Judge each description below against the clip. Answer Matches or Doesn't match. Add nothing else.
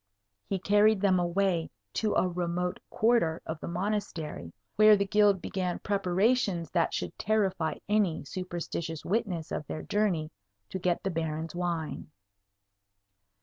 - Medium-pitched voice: Matches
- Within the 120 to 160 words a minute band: Matches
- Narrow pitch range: Doesn't match